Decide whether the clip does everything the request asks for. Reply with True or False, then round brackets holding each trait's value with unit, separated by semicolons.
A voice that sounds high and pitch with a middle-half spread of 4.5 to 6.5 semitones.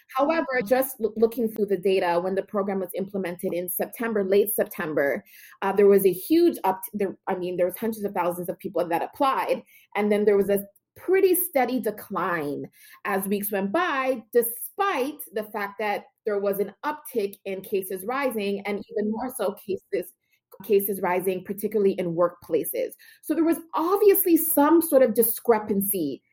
True (210 Hz; 5.2 semitones)